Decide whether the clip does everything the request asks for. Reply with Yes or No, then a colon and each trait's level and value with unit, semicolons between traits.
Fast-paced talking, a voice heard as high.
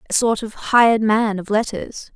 No: average, 195 wpm; high, 215 Hz